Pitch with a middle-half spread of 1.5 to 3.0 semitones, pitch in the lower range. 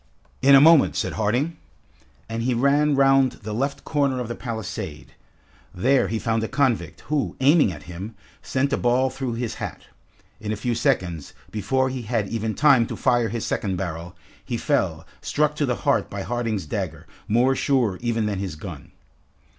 No: average, 4.1 semitones; low, 120 Hz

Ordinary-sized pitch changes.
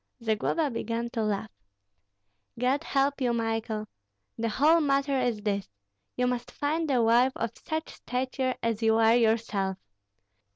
Yes: average, 3.5 semitones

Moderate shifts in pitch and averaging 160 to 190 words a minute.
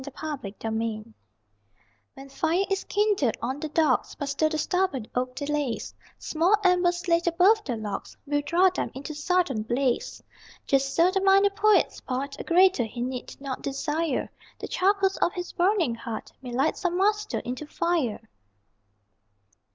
No: wide, 6.1 semitones; average, 165 wpm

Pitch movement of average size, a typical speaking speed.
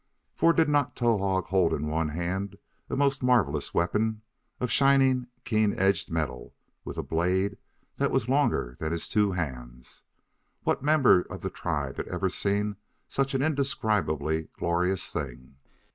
No: wide, 7.6 semitones; average, 150 wpm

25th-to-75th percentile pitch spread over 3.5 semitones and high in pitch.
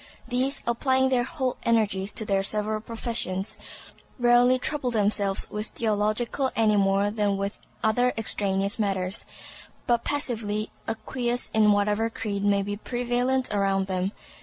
No: average, 3.2 semitones; high, 215 Hz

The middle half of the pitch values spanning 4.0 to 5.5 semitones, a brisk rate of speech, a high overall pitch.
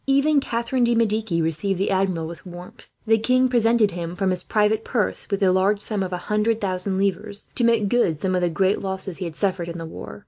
No: average, 3.6 semitones; fast, 235 wpm; high, 195 Hz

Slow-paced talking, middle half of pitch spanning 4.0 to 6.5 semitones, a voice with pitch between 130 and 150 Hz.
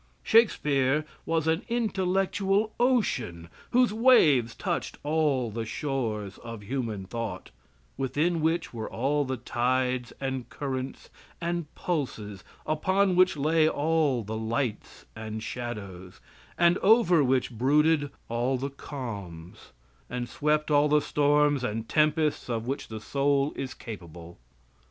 Yes: slow, 125 wpm; wide, 5.5 semitones; low, 135 Hz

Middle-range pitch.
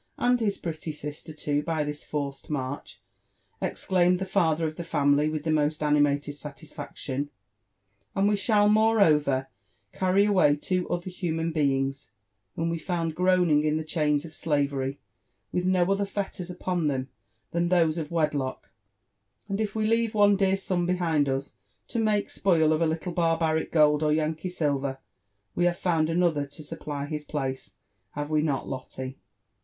Yes: medium, 160 Hz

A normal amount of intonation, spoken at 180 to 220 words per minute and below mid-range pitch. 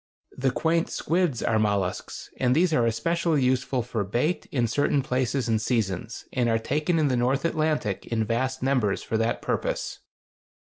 No: average, 4.7 semitones; average, 170 wpm; low, 125 Hz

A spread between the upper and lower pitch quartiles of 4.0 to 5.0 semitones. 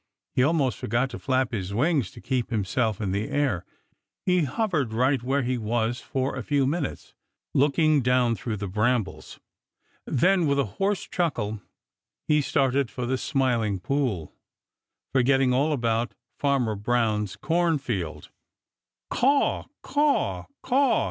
Yes: average, 4.4 semitones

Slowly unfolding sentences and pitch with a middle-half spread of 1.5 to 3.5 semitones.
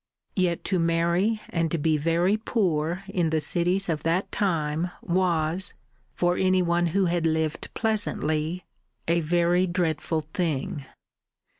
Yes: slow, 130 wpm; narrow, 2.4 semitones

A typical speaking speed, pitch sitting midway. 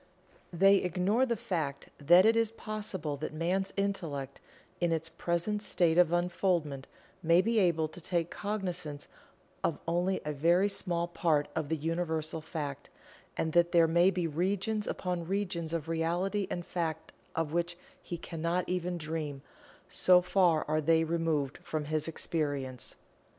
Yes: average, 150 wpm; medium, 170 Hz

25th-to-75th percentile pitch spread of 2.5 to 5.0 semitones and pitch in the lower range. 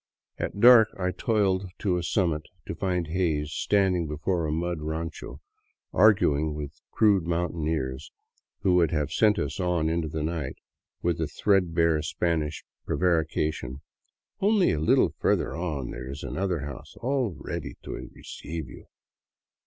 Yes: average, 3.5 semitones; very low, 85 Hz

